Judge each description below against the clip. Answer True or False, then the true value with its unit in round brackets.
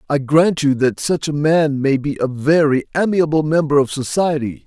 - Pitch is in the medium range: True (145 Hz)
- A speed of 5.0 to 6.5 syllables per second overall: False (4.8 syllables/s)